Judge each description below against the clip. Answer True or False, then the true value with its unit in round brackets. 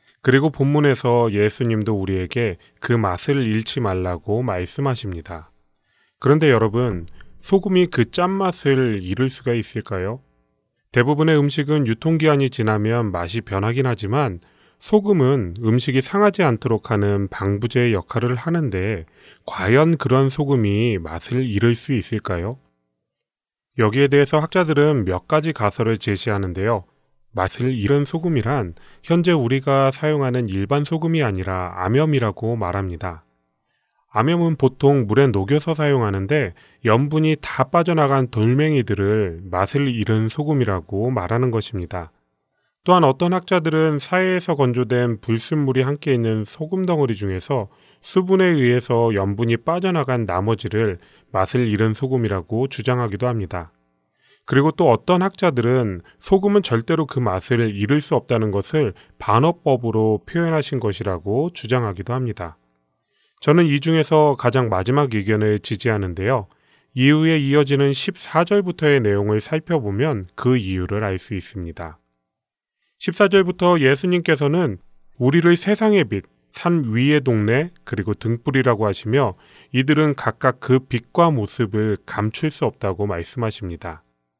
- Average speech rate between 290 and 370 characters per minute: True (305 characters per minute)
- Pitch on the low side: True (120 Hz)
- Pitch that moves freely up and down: True (6.4 semitones)